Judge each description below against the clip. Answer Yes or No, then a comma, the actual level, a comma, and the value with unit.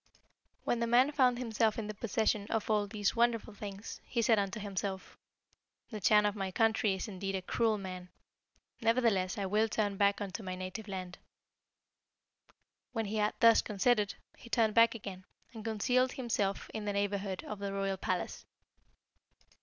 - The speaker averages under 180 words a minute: Yes, average, 170 wpm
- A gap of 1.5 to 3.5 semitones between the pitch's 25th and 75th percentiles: Yes, narrow, 2.5 semitones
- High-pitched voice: Yes, high, 210 Hz